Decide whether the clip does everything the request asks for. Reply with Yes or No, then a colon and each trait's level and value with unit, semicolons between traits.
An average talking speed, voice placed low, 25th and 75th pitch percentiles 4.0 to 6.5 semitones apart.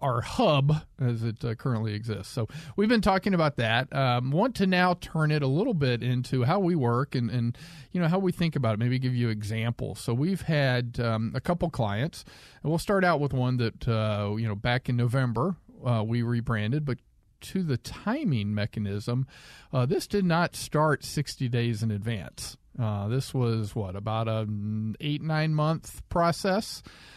Yes: average, 190 wpm; low, 130 Hz; average, 5.2 semitones